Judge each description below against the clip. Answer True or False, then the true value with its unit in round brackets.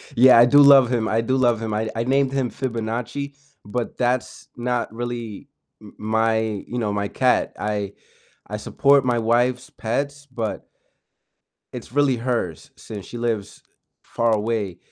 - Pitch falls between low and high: False (120 Hz)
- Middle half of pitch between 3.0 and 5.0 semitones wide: False (2.6 semitones)